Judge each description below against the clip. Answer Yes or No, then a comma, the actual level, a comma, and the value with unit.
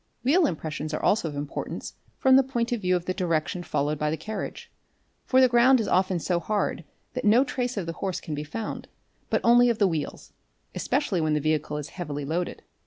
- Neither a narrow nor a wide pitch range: No, wide, 7.3 semitones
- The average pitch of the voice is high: No, medium, 180 Hz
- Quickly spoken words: Yes, fast, 215 wpm